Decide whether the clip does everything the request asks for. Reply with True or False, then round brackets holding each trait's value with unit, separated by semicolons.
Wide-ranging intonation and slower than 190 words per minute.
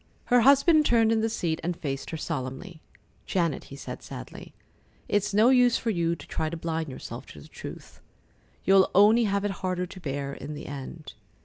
False (6.5 semitones; 195 wpm)